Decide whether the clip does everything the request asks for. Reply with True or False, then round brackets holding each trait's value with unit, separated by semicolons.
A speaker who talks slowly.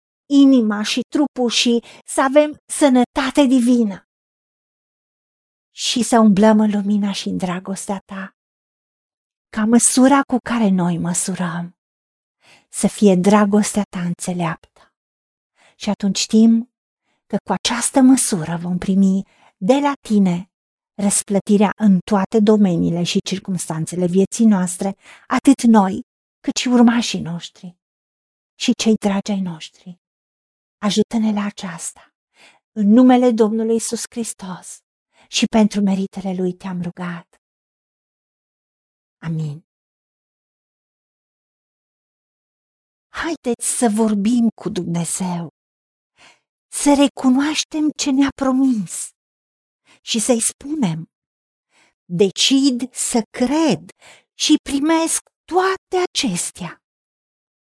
True (100 wpm)